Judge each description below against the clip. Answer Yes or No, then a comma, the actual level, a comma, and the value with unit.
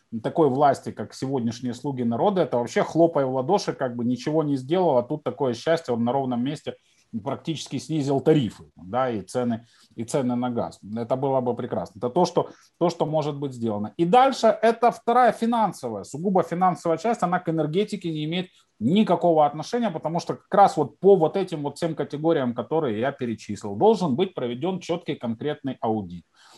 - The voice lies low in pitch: No, medium, 155 Hz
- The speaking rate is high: Yes, fast, 185 wpm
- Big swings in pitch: Yes, wide, 6.2 semitones